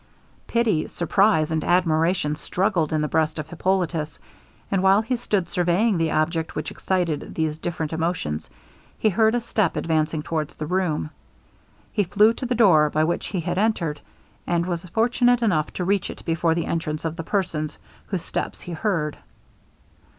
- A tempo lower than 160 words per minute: No, average, 170 wpm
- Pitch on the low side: No, medium, 170 Hz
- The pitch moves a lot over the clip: No, average, 3.9 semitones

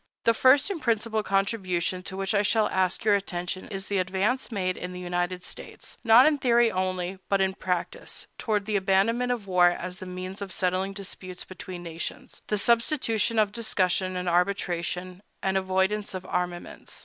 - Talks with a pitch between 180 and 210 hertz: Yes, high, 190 Hz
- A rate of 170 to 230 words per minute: Yes, average, 180 wpm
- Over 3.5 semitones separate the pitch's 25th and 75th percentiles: No, average, 3.0 semitones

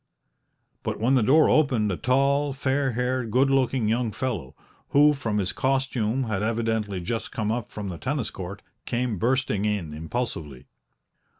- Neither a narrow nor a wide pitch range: Yes, average, 4.1 semitones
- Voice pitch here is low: Yes, low, 120 Hz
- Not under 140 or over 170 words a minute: Yes, average, 160 wpm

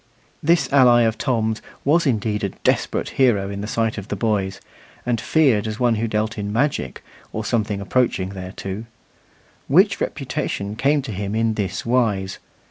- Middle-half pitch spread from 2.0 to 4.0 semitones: Yes, average, 3.1 semitones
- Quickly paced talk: No, average, 165 wpm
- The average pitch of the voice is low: Yes, low, 110 Hz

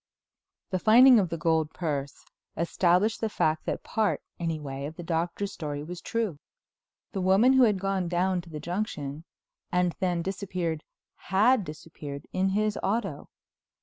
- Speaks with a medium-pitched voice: Yes, medium, 180 Hz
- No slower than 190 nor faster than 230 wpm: No, average, 150 wpm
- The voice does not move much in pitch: No, average, 3.9 semitones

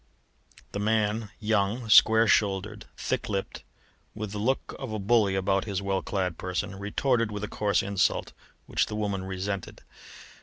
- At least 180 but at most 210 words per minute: No, average, 155 wpm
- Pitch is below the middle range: Yes, low, 105 Hz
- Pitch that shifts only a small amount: Yes, narrow, 1.9 semitones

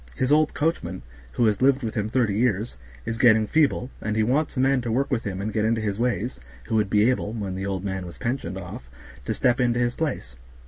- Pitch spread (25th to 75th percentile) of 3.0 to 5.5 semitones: Yes, average, 3.8 semitones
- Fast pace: Yes, fast, 240 wpm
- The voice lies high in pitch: No, low, 115 Hz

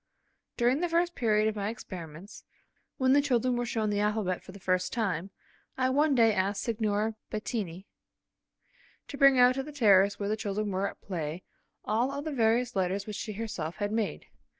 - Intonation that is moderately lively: Yes, average, 3.9 semitones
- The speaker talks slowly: No, average, 190 wpm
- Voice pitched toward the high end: Yes, high, 215 Hz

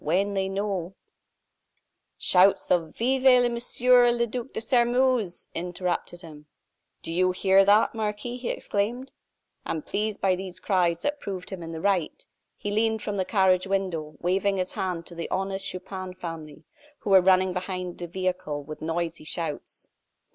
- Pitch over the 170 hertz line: Yes, high, 190 Hz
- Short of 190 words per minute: Yes, average, 160 wpm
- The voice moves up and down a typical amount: Yes, average, 3.2 semitones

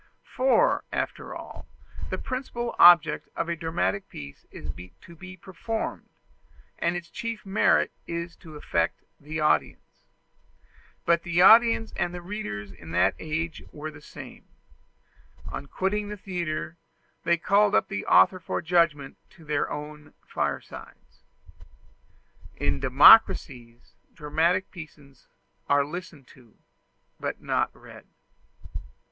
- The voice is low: No, medium, 170 Hz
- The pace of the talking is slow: Yes, slow, 125 wpm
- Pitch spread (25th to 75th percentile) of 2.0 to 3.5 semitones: No, average, 4.3 semitones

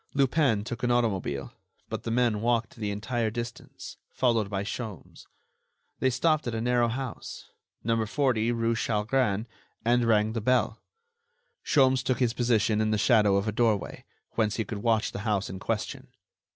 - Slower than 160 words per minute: No, average, 165 wpm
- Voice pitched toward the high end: No, low, 115 Hz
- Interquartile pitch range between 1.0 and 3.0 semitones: Yes, narrow, 2.4 semitones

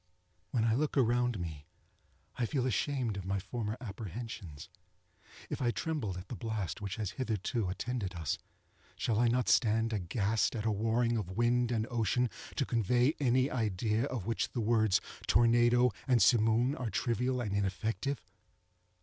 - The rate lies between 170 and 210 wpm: No, average, 160 wpm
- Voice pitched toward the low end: Yes, low, 115 Hz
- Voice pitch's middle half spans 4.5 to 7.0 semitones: No, average, 3.0 semitones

